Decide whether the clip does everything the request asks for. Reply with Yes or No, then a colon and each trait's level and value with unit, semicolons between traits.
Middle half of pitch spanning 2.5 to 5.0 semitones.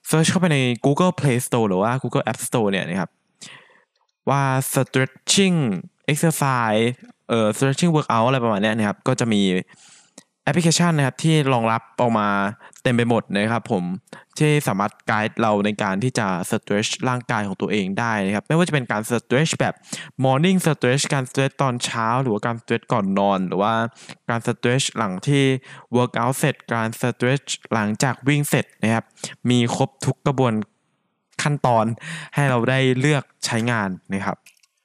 Yes: average, 4.5 semitones